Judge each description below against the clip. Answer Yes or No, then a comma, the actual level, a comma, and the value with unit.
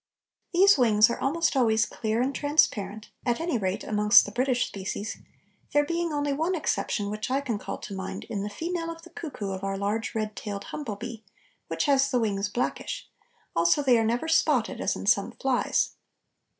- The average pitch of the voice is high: Yes, high, 235 Hz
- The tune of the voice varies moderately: No, wide, 5.8 semitones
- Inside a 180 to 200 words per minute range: Yes, average, 190 wpm